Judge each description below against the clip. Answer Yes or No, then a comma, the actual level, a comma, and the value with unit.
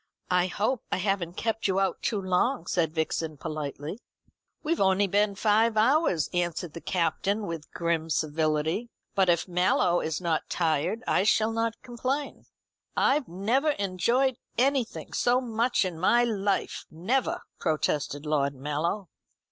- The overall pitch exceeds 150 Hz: Yes, high, 190 Hz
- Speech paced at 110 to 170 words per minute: Yes, average, 140 wpm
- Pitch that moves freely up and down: Yes, wide, 5.7 semitones